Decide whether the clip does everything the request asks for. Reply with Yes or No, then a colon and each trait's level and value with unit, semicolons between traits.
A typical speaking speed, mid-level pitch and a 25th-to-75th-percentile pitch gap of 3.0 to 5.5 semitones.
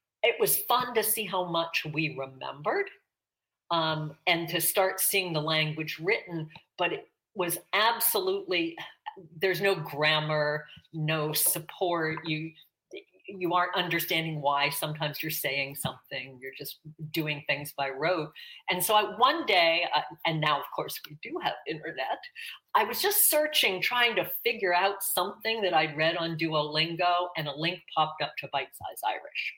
Yes: average, 160 wpm; medium, 170 Hz; average, 4.3 semitones